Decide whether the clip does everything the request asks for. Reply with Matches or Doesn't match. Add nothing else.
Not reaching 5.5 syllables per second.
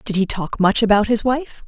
Matches